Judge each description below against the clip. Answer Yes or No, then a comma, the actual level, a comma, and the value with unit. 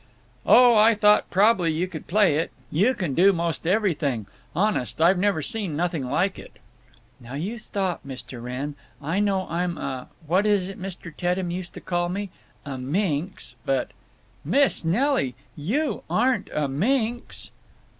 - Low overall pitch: No, medium, 180 Hz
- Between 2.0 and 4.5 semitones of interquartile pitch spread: No, wide, 5.5 semitones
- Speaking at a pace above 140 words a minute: Yes, average, 155 wpm